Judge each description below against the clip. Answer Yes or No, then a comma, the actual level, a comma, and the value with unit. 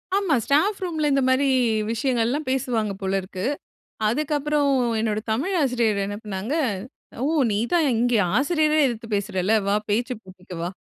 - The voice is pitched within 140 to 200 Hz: No, high, 245 Hz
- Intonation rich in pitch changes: Yes, wide, 6.3 semitones